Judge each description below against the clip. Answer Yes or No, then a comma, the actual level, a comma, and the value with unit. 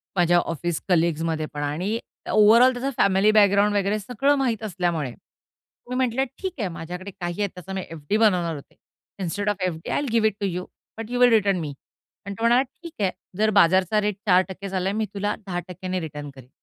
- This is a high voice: Yes, high, 195 Hz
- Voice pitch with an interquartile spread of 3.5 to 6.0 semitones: Yes, average, 3.8 semitones